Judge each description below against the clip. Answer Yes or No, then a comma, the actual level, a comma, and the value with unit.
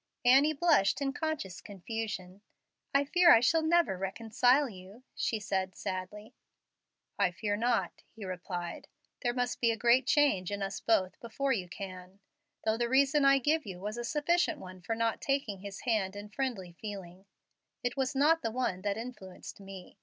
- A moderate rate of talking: Yes, average, 175 wpm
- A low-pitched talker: No, high, 225 Hz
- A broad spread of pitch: Yes, wide, 5.9 semitones